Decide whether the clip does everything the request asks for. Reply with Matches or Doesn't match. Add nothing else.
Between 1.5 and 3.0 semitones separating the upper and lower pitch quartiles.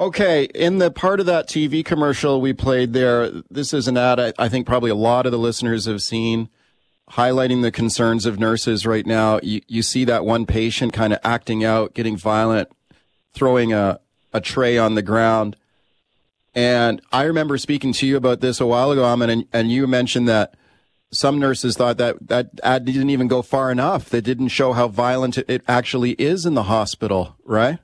Matches